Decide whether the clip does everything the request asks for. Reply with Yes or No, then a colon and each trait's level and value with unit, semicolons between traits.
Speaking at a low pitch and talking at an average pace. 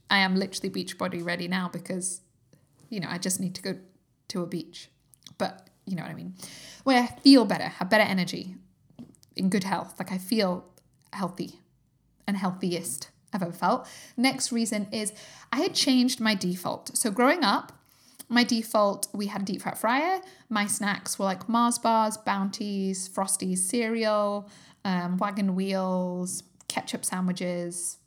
No: high, 195 Hz; average, 165 wpm